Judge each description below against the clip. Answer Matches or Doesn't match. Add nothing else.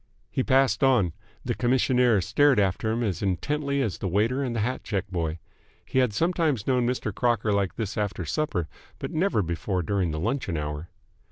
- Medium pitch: Doesn't match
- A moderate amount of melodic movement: Doesn't match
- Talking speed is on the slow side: Doesn't match